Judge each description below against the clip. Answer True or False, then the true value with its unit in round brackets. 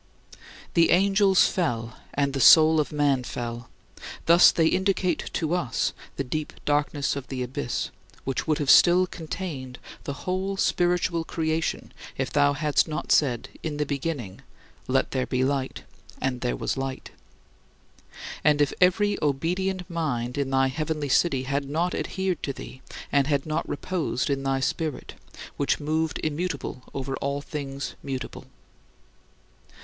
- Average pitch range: True (3.7 semitones)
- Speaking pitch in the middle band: True (145 Hz)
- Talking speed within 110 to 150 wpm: True (145 wpm)